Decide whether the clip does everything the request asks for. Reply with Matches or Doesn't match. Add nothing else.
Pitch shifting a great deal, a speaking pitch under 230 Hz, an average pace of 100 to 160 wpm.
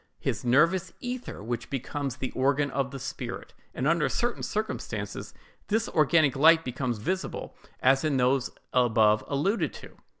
Doesn't match